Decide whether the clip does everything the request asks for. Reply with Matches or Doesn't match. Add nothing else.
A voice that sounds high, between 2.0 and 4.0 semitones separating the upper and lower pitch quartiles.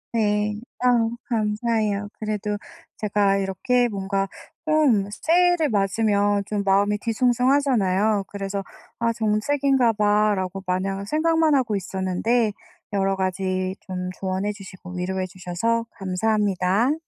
Matches